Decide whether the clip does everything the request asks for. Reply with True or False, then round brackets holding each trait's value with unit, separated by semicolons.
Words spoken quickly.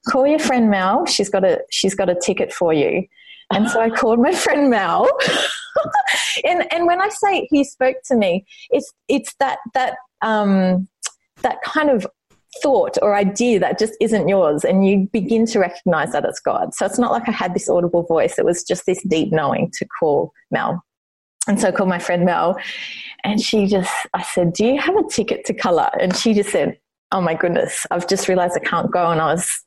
True (210 wpm)